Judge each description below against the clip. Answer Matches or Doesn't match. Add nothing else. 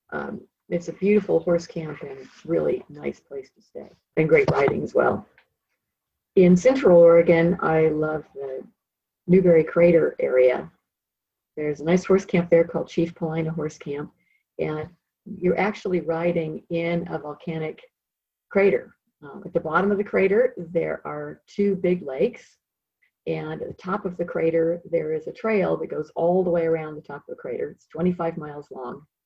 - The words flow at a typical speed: Matches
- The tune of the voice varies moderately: Matches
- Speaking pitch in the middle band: Matches